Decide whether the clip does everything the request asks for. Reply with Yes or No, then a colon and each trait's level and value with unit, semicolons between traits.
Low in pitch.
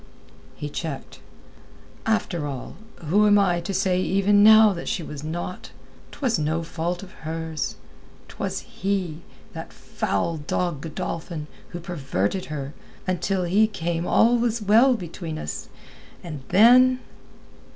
No: medium, 175 Hz